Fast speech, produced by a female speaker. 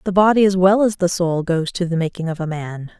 Yes: fast, 280 wpm; female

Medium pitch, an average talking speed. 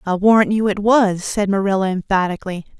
No: high, 200 Hz; average, 170 wpm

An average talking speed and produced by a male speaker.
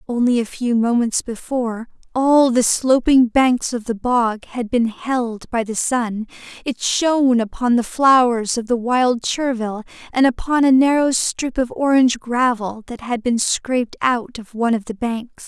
No: average, 175 wpm; female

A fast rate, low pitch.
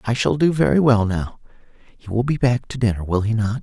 Yes: fast, 250 wpm; low, 115 Hz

